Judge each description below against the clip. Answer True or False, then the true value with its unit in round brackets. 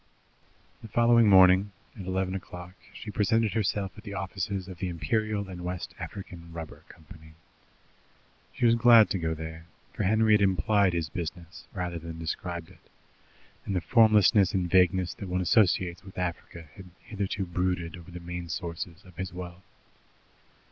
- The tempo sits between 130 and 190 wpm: True (160 wpm)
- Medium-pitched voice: False (90 Hz)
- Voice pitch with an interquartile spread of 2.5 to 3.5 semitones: True (2.8 semitones)